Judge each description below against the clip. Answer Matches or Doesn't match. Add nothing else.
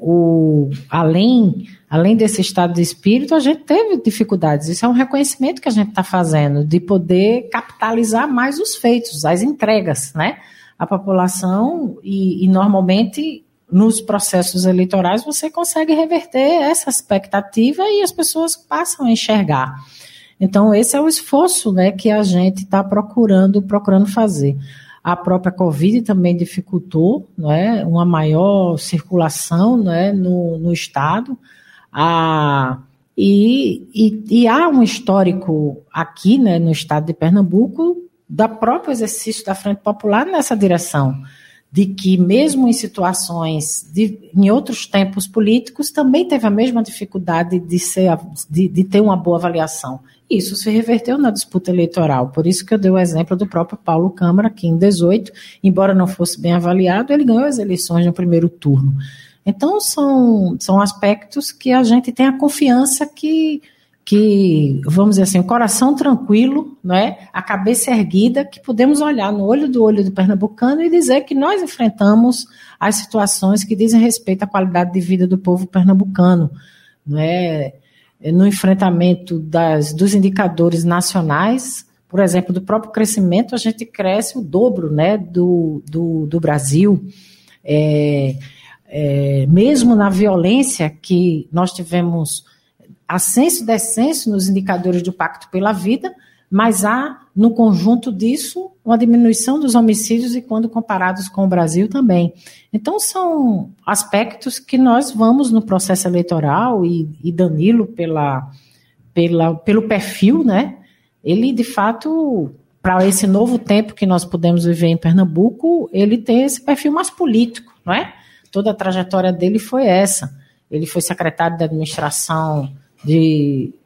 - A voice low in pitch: Doesn't match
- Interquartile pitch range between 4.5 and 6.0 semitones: Matches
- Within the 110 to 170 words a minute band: Matches